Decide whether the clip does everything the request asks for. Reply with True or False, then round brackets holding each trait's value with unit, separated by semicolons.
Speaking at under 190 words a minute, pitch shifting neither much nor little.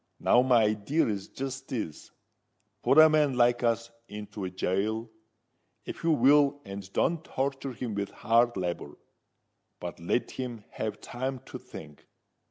True (140 wpm; 4.6 semitones)